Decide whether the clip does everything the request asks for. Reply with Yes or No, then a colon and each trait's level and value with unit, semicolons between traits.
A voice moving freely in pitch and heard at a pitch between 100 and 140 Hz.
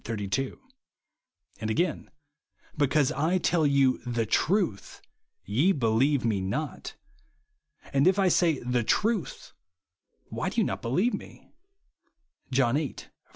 Yes: wide, 6.2 semitones; low, 135 Hz